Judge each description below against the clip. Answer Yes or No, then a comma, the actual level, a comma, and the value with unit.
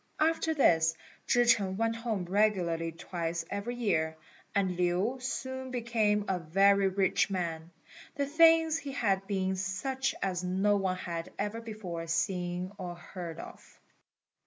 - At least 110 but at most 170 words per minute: Yes, average, 140 wpm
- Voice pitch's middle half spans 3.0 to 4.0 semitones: No, average, 4.7 semitones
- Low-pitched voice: No, high, 195 Hz